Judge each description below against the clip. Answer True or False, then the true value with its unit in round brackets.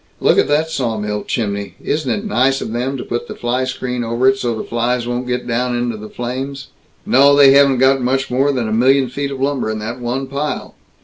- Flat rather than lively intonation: True (2.3 semitones)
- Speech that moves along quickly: True (230 wpm)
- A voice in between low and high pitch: False (125 Hz)